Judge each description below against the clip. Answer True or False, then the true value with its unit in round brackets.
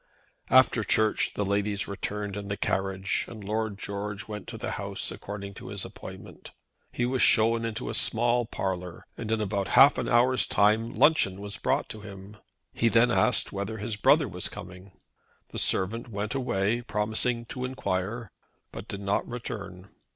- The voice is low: True (105 Hz)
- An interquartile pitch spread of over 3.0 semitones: False (2.7 semitones)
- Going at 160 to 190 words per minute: True (170 wpm)